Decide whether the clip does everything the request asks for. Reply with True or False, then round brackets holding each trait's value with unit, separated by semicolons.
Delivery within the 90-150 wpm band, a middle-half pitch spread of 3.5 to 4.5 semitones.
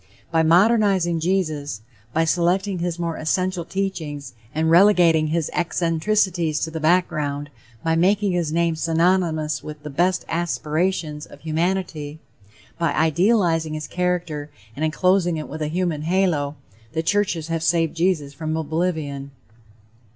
False (135 wpm; 2.5 semitones)